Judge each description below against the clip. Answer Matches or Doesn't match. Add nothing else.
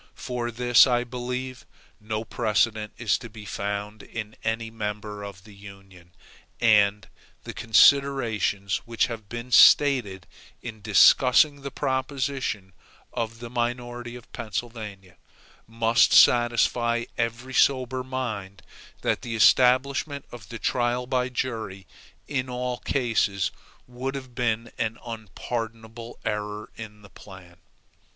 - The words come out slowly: Matches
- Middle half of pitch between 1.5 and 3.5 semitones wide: Matches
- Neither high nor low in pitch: Doesn't match